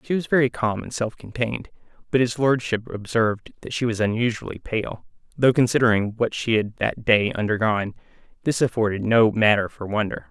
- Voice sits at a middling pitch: No, low, 110 Hz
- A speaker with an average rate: Yes, average, 170 wpm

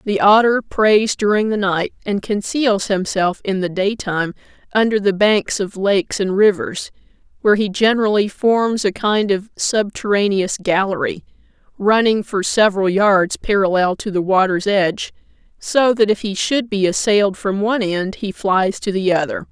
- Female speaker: Yes, female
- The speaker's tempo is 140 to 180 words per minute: Yes, average, 160 wpm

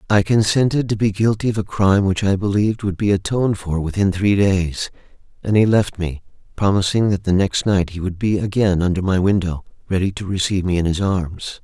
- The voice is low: Yes, low, 100 Hz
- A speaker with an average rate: No, fast, 210 wpm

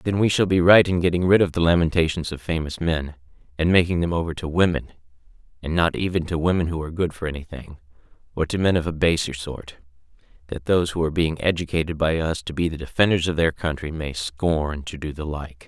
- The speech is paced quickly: Yes, fast, 220 wpm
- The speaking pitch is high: No, very low, 80 Hz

